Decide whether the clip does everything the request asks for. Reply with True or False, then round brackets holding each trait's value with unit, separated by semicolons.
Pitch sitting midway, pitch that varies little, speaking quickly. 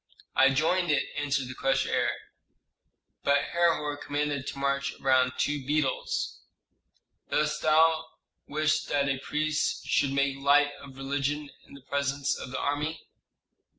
False (145 Hz; 1.7 semitones; 140 wpm)